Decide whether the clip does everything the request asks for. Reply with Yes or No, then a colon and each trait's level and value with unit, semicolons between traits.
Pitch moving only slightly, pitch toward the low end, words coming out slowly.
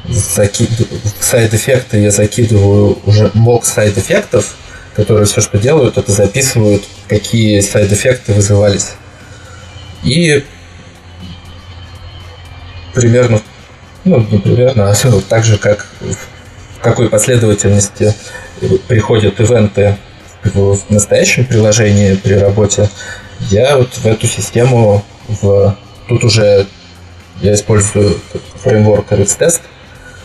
Yes: narrow, 2.0 semitones; low, 105 Hz; slow, 100 wpm